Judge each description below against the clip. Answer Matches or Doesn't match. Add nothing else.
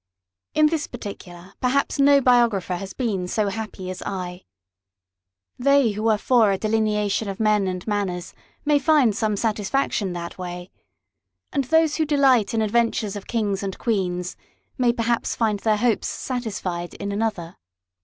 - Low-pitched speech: Doesn't match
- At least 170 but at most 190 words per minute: Doesn't match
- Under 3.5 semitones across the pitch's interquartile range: Doesn't match